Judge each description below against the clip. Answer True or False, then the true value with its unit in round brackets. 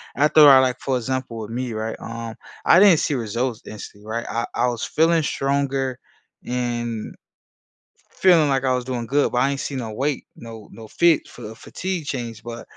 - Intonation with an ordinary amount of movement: True (3.4 semitones)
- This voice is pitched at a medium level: False (125 Hz)